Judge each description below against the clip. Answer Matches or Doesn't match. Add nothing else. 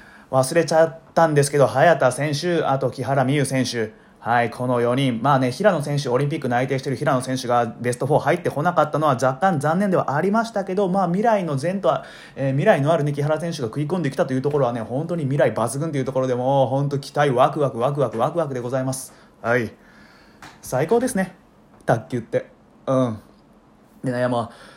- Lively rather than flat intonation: Doesn't match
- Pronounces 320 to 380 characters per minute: Doesn't match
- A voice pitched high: Doesn't match